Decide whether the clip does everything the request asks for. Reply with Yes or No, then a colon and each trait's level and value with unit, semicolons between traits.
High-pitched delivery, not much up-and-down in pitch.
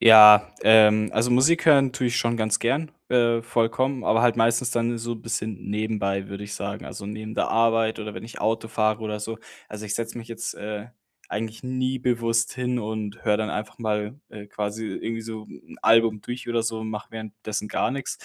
No: low, 110 Hz; narrow, 1.7 semitones